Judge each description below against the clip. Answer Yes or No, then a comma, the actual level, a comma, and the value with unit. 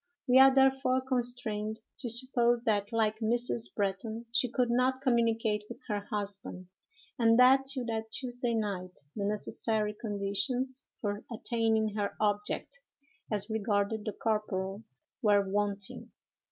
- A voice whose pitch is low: No, high, 220 Hz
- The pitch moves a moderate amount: Yes, average, 3.0 semitones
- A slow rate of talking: Yes, slow, 130 wpm